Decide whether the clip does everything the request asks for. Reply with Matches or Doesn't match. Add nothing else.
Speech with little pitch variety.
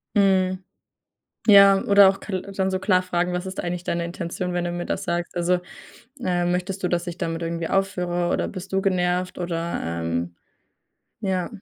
Matches